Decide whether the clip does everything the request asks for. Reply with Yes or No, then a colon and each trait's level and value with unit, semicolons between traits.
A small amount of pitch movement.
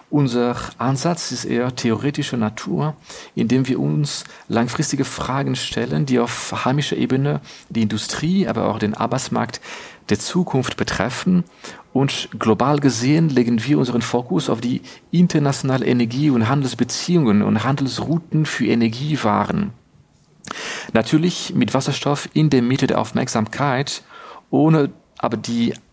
No: average, 3.8 semitones